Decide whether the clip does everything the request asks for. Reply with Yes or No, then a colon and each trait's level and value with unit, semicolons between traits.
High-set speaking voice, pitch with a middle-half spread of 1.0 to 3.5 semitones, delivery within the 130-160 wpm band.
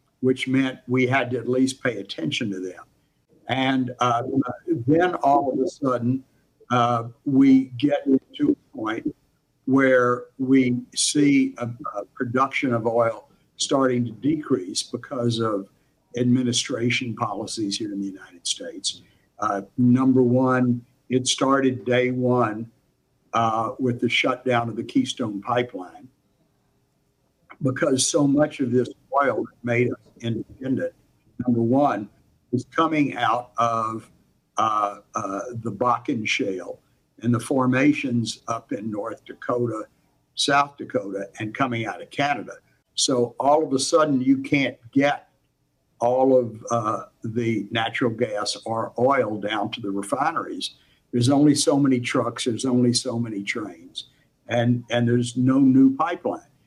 No: low, 125 Hz; narrow, 2.4 semitones; average, 140 wpm